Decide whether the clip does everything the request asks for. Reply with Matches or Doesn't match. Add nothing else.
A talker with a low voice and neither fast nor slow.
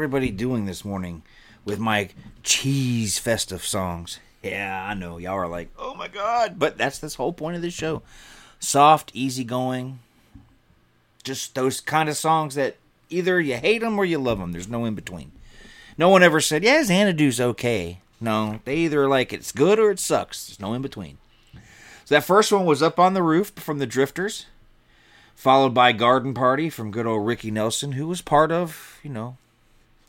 Matches